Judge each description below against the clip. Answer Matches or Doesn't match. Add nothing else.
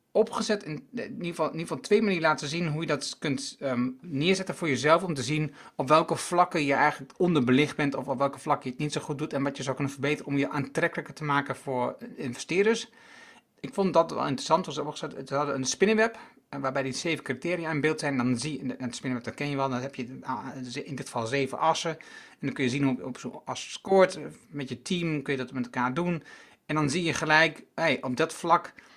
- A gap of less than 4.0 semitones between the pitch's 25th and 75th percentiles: Matches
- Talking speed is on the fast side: Matches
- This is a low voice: Doesn't match